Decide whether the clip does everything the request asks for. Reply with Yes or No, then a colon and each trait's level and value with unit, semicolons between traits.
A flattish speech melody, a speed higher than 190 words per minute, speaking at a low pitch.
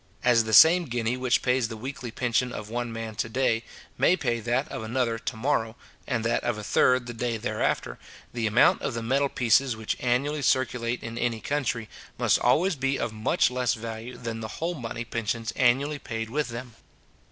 Yes: narrow, 2.2 semitones; average, 200 wpm; low, 120 Hz